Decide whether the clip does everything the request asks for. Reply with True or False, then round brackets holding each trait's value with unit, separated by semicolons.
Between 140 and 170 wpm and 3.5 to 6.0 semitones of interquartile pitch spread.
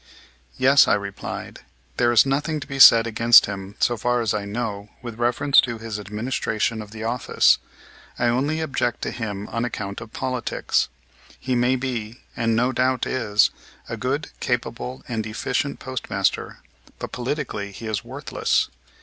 False (160 wpm; 3.0 semitones)